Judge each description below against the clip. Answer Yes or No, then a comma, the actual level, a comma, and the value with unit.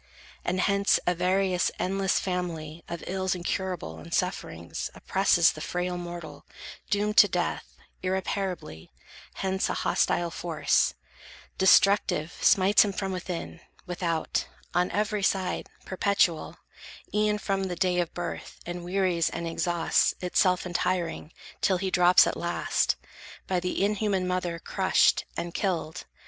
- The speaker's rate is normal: No, slow, 130 wpm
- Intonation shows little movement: Yes, narrow, 1.8 semitones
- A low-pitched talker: No, medium, 180 Hz